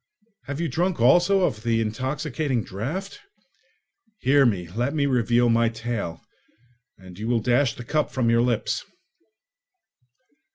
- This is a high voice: No, low, 120 Hz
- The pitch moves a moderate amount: Yes, average, 4.1 semitones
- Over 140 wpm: No, slow, 135 wpm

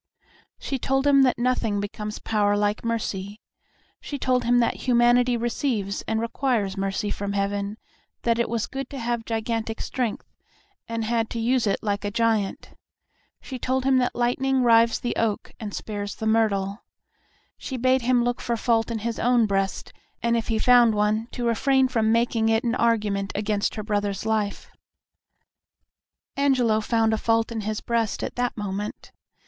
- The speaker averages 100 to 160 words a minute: No, average, 170 wpm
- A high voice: Yes, high, 225 Hz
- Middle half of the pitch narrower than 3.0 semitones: Yes, narrow, 2.6 semitones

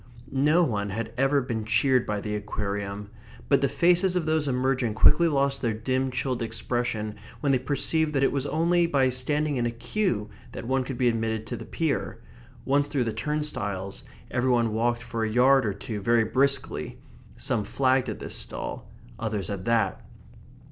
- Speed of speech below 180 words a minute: No, average, 185 wpm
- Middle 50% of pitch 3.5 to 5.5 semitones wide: Yes, average, 4.0 semitones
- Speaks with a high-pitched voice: No, low, 125 Hz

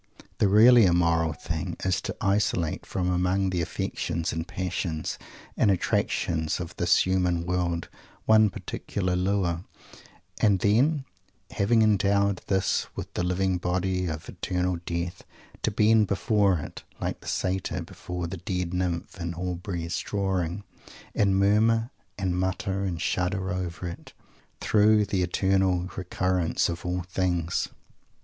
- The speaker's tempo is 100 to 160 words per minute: Yes, slow, 135 wpm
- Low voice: Yes, very low, 90 Hz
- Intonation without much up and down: Yes, narrow, 2.0 semitones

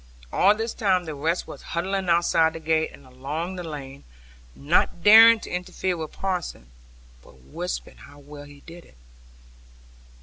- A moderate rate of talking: Yes, average, 160 wpm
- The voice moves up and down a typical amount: Yes, average, 4.1 semitones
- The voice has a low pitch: No, medium, 165 Hz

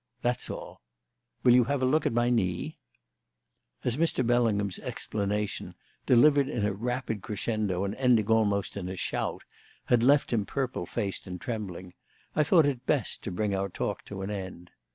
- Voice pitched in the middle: No, low, 110 Hz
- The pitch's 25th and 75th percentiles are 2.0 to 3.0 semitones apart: No, average, 4.2 semitones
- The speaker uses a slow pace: No, average, 175 wpm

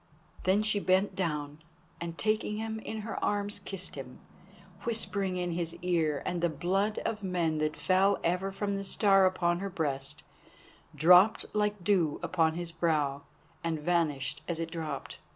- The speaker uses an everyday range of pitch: Yes, average, 3.7 semitones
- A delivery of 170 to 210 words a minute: No, average, 160 wpm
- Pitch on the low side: No, medium, 180 Hz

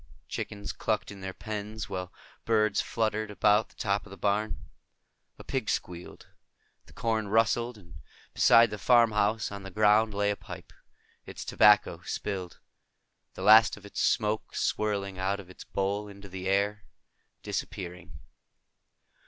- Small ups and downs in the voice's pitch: Yes, narrow, 1.6 semitones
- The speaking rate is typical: Yes, average, 145 wpm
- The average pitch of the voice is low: Yes, low, 105 Hz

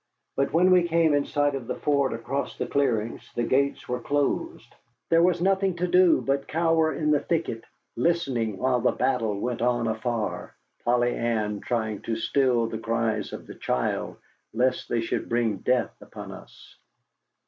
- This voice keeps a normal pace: Yes, average, 170 wpm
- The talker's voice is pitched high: No, low, 130 Hz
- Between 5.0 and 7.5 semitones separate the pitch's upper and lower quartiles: Yes, wide, 5.4 semitones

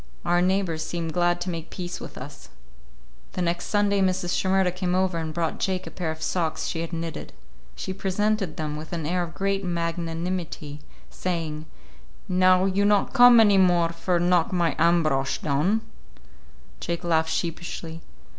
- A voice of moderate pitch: Yes, medium, 175 Hz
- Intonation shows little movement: Yes, narrow, 2.3 semitones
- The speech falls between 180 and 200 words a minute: No, average, 165 wpm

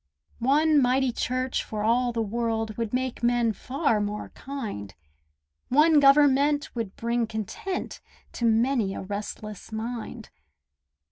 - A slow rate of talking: Yes, slow, 125 wpm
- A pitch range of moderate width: Yes, average, 3.5 semitones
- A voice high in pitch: Yes, high, 235 Hz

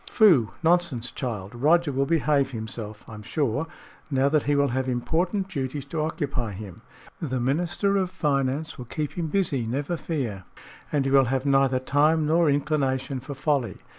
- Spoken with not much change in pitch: No, average, 3.8 semitones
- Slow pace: No, average, 170 wpm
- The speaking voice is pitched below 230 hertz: Yes, medium, 140 Hz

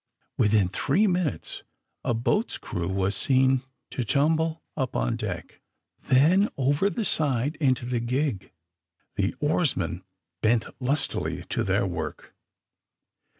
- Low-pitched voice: Yes, low, 130 Hz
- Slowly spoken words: Yes, slow, 120 wpm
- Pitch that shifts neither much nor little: No, wide, 5.9 semitones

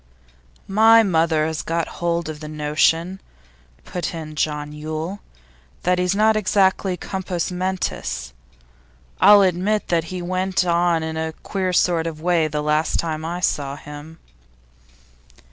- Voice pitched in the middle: Yes, medium, 170 Hz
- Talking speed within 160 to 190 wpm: No, average, 140 wpm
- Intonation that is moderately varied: Yes, average, 3.0 semitones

